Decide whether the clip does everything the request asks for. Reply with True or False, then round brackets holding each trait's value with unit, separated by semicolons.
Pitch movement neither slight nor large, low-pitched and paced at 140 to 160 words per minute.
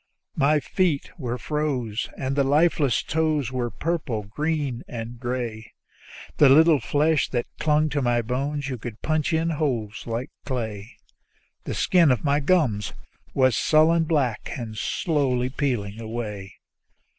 True (4.5 semitones; 130 Hz; 150 wpm)